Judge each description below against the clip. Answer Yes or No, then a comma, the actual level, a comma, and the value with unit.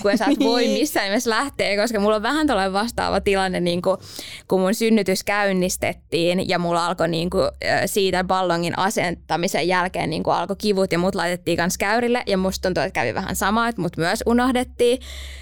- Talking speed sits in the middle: No, fast, 185 wpm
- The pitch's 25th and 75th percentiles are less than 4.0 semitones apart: Yes, average, 3.6 semitones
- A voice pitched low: No, high, 195 Hz